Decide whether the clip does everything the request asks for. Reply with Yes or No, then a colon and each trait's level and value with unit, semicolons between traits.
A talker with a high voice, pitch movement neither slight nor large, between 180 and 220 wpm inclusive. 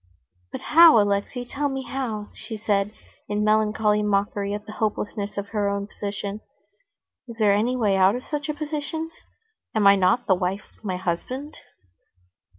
No: high, 210 Hz; average, 3.7 semitones; average, 165 wpm